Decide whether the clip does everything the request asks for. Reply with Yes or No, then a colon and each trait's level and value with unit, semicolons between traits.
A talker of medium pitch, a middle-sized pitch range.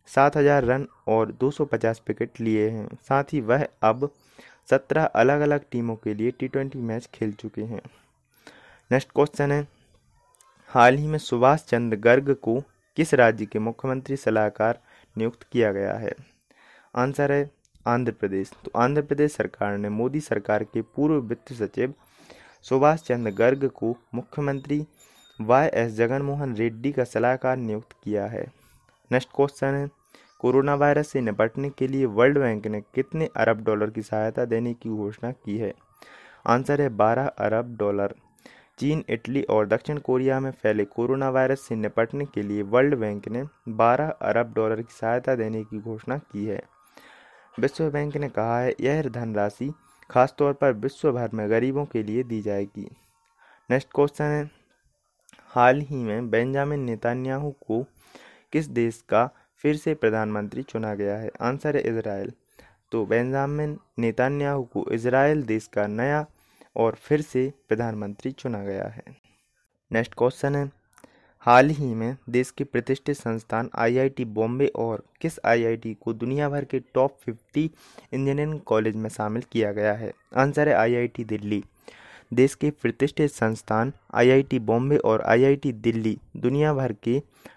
No: low, 125 Hz; average, 3.8 semitones